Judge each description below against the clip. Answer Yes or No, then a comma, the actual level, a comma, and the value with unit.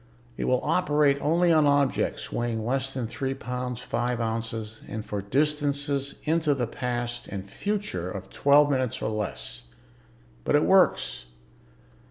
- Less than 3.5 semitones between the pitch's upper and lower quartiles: No, average, 4.4 semitones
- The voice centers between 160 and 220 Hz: No, low, 130 Hz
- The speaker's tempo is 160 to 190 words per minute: No, average, 145 wpm